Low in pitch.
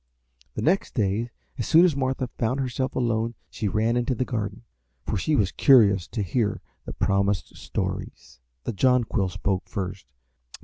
Yes: low, 115 Hz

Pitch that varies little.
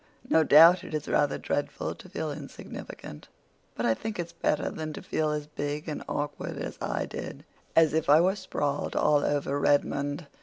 Yes: narrow, 1.8 semitones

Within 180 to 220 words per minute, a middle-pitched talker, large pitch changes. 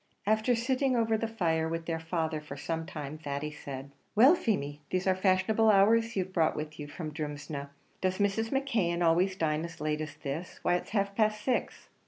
Yes: average, 195 wpm; medium, 175 Hz; wide, 5.8 semitones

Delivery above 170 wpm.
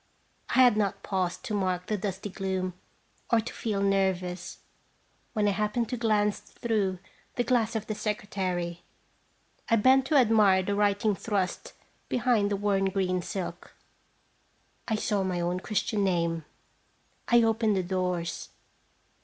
No: average, 145 wpm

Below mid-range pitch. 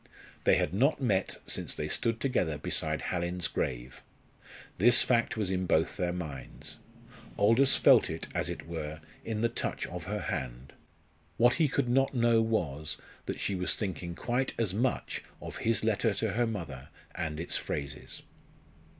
Yes: low, 100 Hz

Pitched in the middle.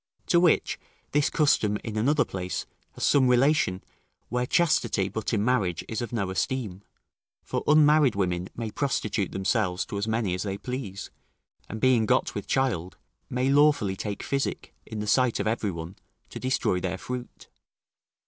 No: low, 110 Hz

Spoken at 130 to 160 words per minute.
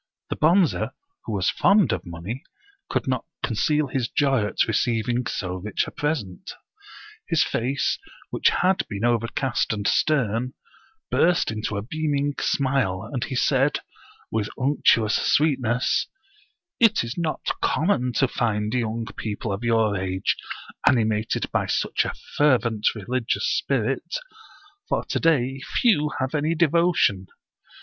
Yes: average, 140 wpm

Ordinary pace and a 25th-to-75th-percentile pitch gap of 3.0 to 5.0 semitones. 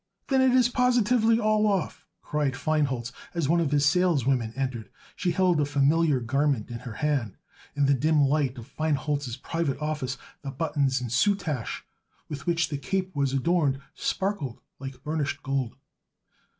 Yes: average, 165 wpm; average, 4.3 semitones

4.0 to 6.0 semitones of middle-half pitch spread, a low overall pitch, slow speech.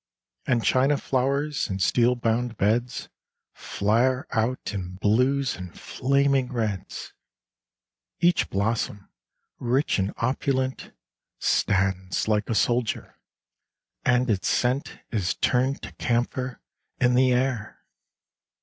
No: average, 3.6 semitones; low, 125 Hz; slow, 105 wpm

